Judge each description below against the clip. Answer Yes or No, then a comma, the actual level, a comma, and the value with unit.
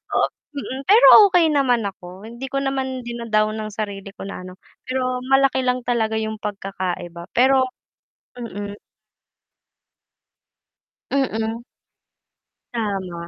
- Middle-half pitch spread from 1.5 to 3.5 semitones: No, average, 4.4 semitones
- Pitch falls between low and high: No, high, 225 Hz